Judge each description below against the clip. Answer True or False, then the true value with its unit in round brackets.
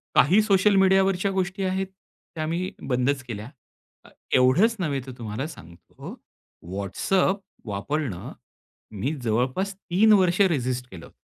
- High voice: False (155 Hz)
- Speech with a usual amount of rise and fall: False (7.5 semitones)